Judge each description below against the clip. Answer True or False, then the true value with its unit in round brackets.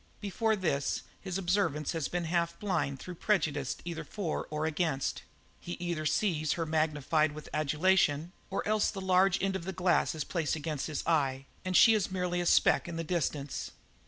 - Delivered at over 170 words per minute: True (185 wpm)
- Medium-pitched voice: True (170 Hz)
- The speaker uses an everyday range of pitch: True (3.5 semitones)